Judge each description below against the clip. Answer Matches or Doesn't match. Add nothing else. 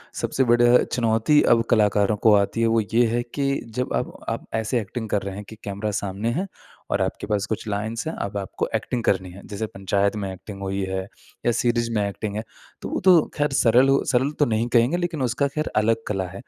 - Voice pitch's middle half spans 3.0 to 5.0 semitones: Matches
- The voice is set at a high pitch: Doesn't match